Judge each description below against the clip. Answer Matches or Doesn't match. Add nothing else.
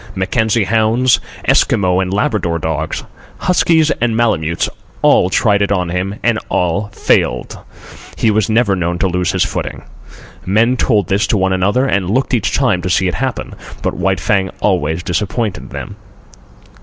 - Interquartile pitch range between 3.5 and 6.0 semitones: Matches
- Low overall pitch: Matches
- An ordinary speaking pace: Matches